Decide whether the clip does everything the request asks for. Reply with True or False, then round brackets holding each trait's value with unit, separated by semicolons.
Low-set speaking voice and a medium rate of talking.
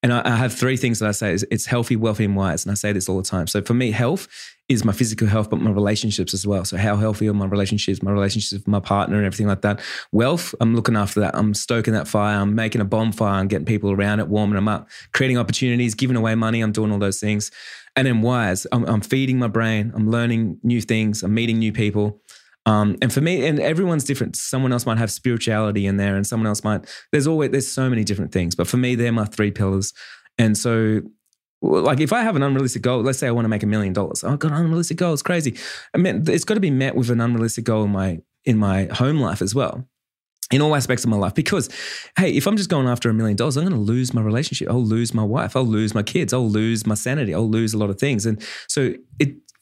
False (110 Hz; 260 wpm)